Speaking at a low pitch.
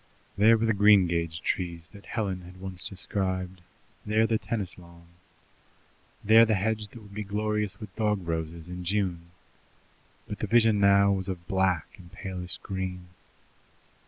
Yes: very low, 95 Hz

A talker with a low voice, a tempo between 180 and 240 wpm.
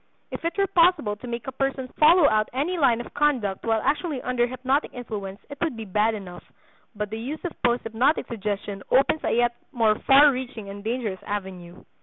No: high, 240 Hz; average, 195 wpm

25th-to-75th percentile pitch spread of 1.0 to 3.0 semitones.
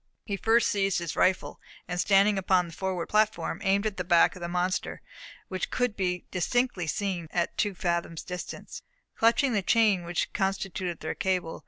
Yes: narrow, 2.5 semitones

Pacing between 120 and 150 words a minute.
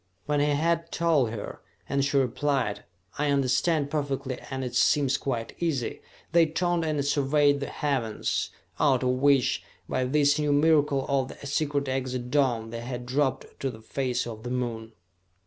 No: average, 165 wpm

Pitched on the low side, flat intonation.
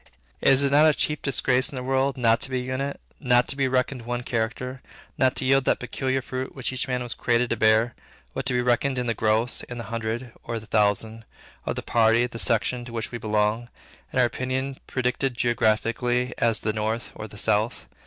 Yes: low, 120 Hz; narrow, 2.3 semitones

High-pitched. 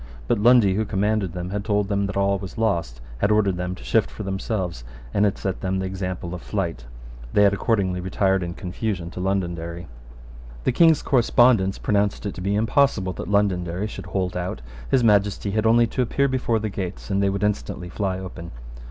No: low, 100 Hz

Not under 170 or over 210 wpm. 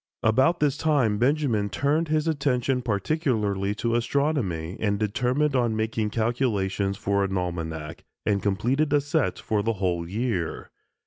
No: average, 140 wpm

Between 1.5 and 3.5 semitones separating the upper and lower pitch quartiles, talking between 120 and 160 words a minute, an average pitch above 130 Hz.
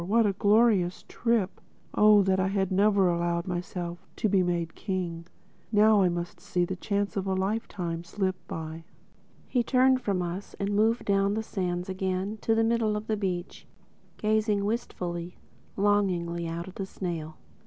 Yes: average, 3.1 semitones; average, 155 wpm; high, 190 Hz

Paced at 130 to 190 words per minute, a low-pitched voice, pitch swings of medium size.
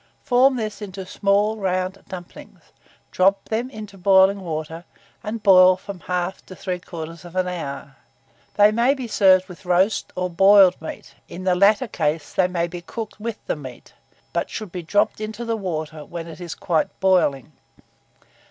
No: average, 160 wpm; medium, 185 Hz; average, 3.0 semitones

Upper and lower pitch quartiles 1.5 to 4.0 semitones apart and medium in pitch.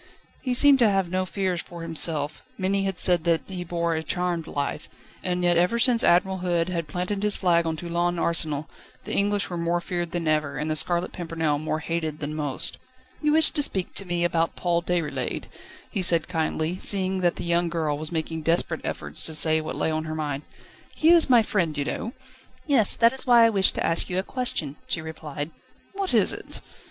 Yes: average, 3.1 semitones; medium, 175 Hz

